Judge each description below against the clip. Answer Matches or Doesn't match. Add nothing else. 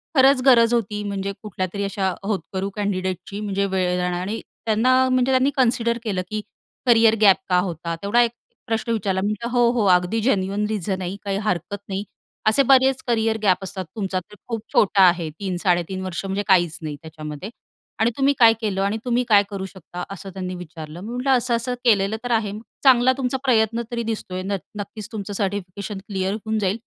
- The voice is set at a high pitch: Matches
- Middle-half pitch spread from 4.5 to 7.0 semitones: Doesn't match